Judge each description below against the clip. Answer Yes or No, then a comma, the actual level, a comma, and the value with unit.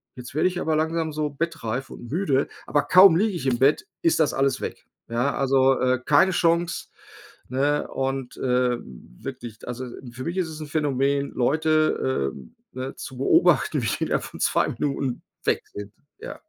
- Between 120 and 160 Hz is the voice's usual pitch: Yes, medium, 140 Hz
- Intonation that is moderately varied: Yes, average, 3.8 semitones